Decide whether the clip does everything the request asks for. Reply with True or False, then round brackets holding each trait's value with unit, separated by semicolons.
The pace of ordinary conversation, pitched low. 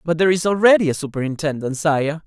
False (185 wpm; 160 Hz)